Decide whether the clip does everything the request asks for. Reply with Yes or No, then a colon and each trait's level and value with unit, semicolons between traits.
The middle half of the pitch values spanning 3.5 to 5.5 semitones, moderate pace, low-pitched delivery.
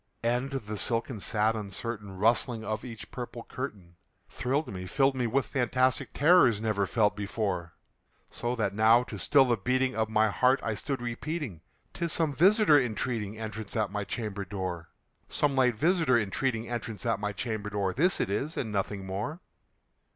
Yes: average, 3.9 semitones; average, 170 wpm; low, 115 Hz